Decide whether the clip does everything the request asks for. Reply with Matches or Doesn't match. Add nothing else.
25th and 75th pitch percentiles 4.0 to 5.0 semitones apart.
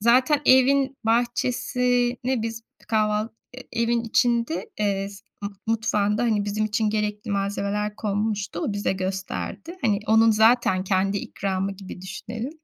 Doesn't match